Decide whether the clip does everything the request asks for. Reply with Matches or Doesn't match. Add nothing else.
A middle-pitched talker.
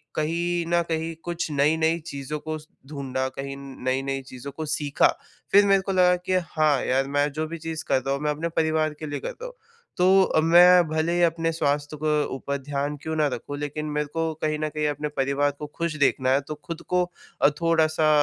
Matches